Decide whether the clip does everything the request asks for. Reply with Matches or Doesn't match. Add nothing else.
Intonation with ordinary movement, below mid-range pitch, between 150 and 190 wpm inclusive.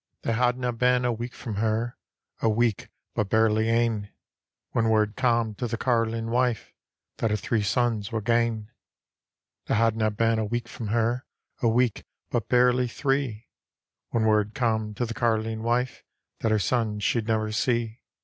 Doesn't match